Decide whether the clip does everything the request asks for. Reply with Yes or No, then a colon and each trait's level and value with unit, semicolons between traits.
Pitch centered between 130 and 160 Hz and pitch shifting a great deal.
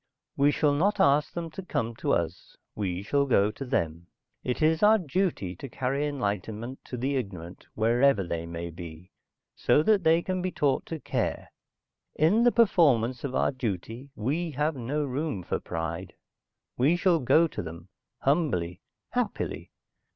Yes: low, 135 Hz; wide, 8.0 semitones